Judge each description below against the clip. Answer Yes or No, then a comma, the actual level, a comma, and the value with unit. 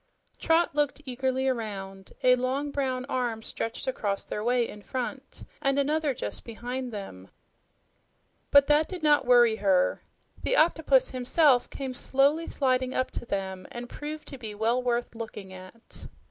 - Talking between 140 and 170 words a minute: Yes, average, 155 wpm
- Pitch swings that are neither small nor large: Yes, average, 3.8 semitones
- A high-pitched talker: Yes, very high, 255 Hz